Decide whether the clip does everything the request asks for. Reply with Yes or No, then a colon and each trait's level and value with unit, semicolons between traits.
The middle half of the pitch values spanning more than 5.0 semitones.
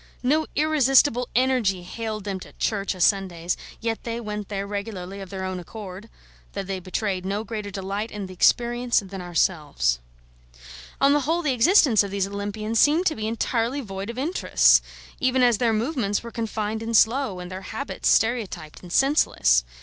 No: average, 4.1 semitones